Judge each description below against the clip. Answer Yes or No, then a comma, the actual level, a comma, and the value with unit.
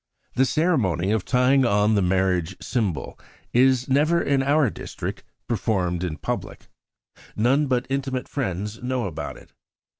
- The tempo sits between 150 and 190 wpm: No, average, 140 wpm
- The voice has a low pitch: Yes, low, 120 Hz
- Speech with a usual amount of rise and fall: No, wide, 5.9 semitones